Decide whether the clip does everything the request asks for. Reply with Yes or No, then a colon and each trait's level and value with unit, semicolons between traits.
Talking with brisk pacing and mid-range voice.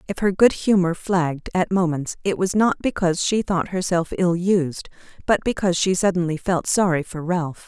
No: average, 190 wpm; medium, 180 Hz